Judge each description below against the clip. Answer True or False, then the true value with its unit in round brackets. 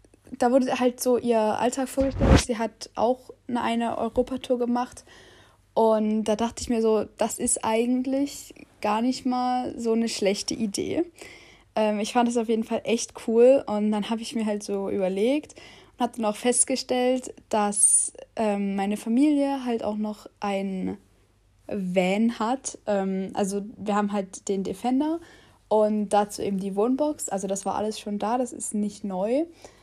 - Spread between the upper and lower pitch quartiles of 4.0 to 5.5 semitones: False (3.4 semitones)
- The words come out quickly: False (170 wpm)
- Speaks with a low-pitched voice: False (225 Hz)